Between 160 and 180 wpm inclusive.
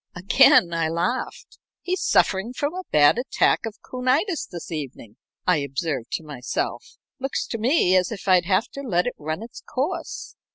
Yes: average, 170 wpm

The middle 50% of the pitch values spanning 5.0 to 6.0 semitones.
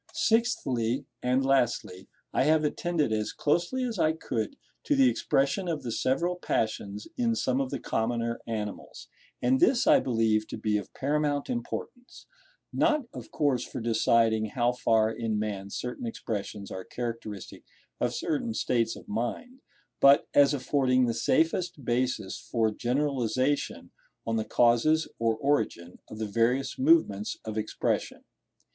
Yes: average, 5.3 semitones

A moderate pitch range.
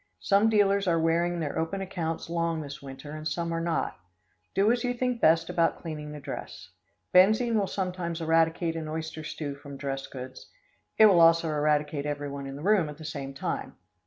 Yes: average, 3.5 semitones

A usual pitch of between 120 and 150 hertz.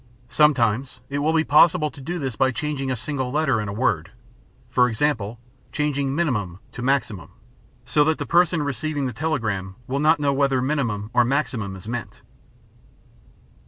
Yes: low, 135 Hz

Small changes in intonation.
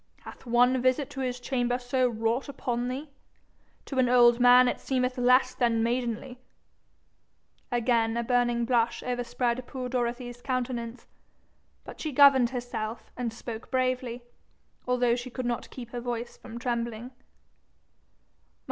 Yes: narrow, 1.2 semitones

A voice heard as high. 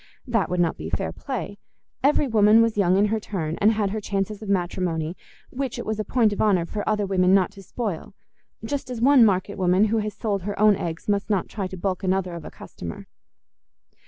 Yes: high, 205 Hz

